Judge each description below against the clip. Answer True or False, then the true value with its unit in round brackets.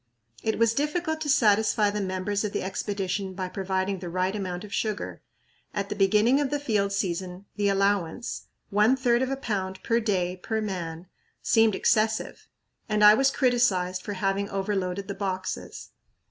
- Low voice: False (200 Hz)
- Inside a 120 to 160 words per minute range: False (170 wpm)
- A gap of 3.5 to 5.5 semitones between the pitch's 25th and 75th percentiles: False (2.8 semitones)